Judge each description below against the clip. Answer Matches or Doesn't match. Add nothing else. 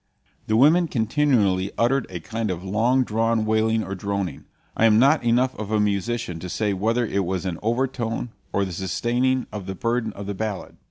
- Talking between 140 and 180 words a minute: Doesn't match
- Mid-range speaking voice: Doesn't match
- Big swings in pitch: Doesn't match